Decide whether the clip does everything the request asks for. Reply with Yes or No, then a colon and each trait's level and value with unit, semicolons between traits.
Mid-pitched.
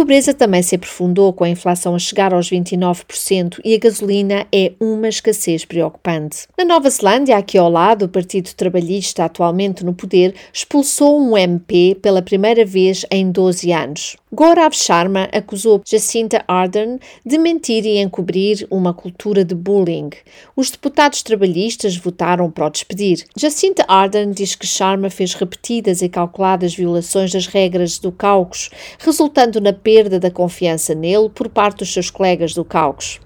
No: high, 195 Hz